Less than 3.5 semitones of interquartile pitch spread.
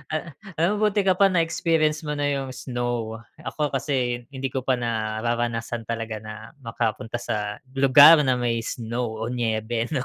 No: average, 4.3 semitones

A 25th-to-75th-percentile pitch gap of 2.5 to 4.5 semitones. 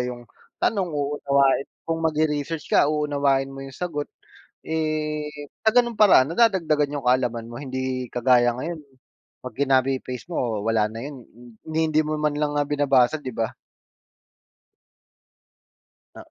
Yes: average, 3.1 semitones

